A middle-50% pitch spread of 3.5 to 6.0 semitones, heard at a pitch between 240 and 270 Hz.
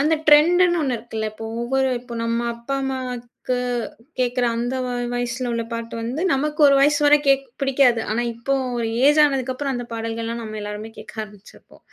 No: average, 2.9 semitones; high, 245 Hz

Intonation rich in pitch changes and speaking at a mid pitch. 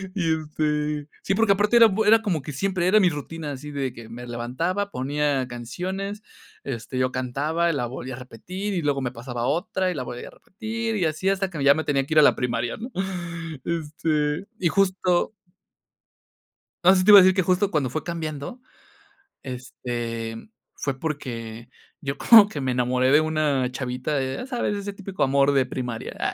Yes: wide, 6.5 semitones; medium, 150 Hz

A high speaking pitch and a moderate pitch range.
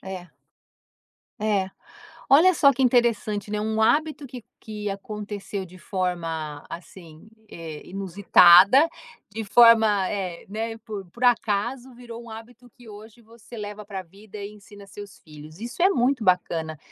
Yes: high, 210 Hz; average, 3.8 semitones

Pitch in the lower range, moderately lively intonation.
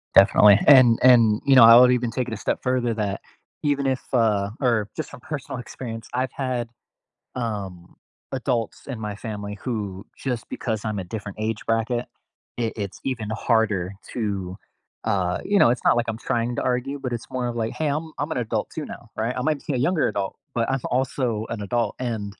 Yes: low, 115 Hz; average, 3.2 semitones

